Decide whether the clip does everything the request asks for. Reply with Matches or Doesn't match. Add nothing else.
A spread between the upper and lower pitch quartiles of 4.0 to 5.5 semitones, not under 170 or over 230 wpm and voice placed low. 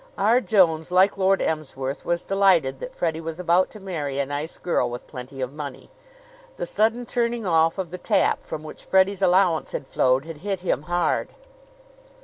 Doesn't match